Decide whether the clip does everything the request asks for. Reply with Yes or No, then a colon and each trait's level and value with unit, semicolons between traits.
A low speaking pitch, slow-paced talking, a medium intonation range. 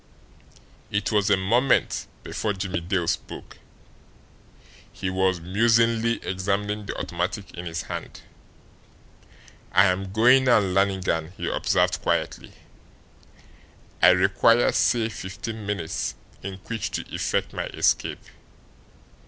Yes: low, 100 Hz; slow, 110 wpm; average, 3.0 semitones